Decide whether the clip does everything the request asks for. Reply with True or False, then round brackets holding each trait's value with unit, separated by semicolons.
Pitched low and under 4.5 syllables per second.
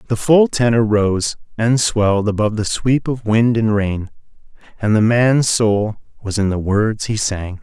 True (110 Hz; 4.2 syllables/s)